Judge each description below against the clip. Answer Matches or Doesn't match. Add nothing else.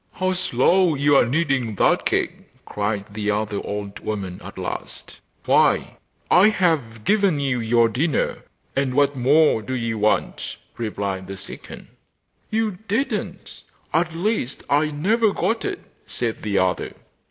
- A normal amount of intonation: Doesn't match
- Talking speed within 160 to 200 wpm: Doesn't match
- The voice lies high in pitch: Doesn't match